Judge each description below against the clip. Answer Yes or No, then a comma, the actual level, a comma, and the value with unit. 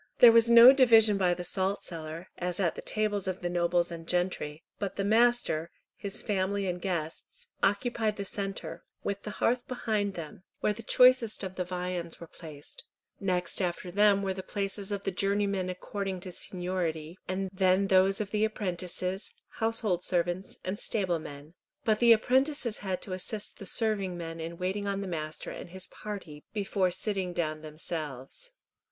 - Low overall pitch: No, high, 190 Hz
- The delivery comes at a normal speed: Yes, average, 170 wpm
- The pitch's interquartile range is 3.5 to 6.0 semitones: No, average, 2.9 semitones